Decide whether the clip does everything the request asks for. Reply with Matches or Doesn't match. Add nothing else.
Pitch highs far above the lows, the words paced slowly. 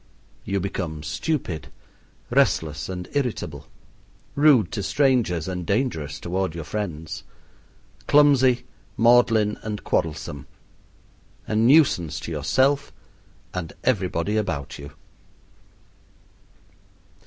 Matches